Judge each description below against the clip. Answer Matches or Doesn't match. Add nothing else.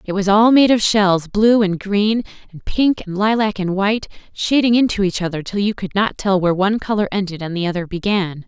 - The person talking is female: Matches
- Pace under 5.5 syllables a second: Doesn't match